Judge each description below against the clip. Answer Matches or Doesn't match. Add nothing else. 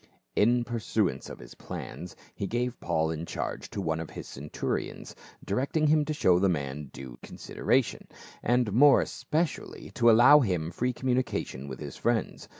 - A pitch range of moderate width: Doesn't match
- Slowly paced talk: Doesn't match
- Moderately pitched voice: Doesn't match